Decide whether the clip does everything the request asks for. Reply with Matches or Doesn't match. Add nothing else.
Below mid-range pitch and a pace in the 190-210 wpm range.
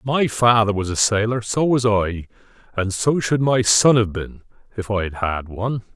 Matches